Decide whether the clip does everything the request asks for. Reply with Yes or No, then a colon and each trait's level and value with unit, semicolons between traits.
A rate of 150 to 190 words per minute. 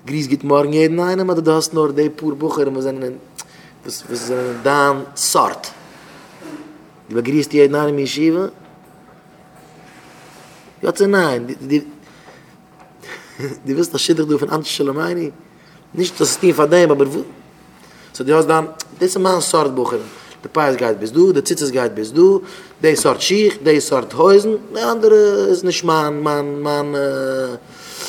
Yes: average, 155 wpm